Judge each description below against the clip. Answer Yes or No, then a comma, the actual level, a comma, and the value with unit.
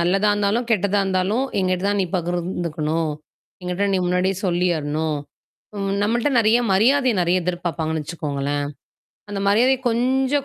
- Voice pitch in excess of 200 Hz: No, medium, 185 Hz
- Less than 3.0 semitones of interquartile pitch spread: No, average, 3.7 semitones